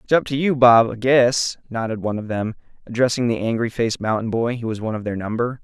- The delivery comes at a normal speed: No, fast, 245 wpm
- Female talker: No, male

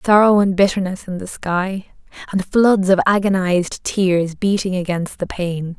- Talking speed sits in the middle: Yes, average, 155 wpm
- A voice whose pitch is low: No, high, 190 Hz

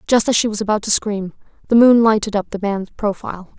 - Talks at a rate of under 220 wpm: No, fast, 235 wpm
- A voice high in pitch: Yes, high, 210 Hz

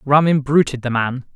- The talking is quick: No, average, 180 wpm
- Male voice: Yes, male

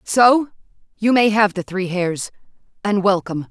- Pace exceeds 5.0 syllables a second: No, 4.6 syllables/s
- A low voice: No, high, 200 Hz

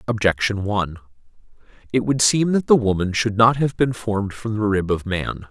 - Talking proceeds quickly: No, average, 195 wpm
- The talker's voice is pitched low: Yes, low, 105 Hz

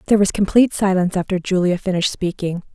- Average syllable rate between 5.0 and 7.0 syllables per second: No, 7.3 syllables/s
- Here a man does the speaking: No, female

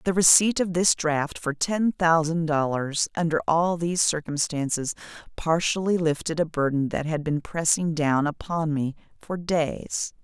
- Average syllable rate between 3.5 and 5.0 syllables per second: Yes, 4.3 syllables/s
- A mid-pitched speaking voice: Yes, medium, 160 Hz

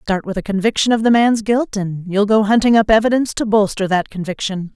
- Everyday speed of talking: No, fast, 225 wpm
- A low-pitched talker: No, high, 210 Hz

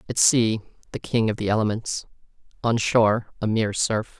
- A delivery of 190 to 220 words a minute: No, average, 170 wpm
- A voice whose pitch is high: No, low, 110 Hz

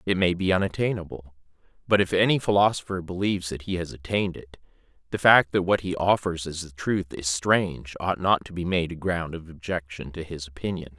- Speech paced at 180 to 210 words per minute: Yes, average, 200 wpm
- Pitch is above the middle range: No, very low, 85 Hz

